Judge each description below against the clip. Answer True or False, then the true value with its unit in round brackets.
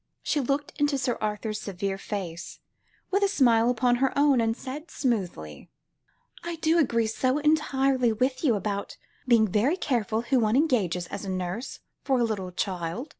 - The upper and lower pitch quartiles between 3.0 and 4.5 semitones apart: False (5.1 semitones)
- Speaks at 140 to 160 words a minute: False (170 wpm)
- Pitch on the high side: True (235 Hz)